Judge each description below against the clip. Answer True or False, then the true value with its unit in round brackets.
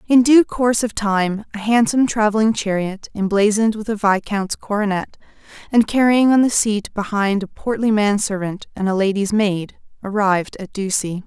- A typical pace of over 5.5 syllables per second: False (5.0 syllables/s)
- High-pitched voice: True (210 Hz)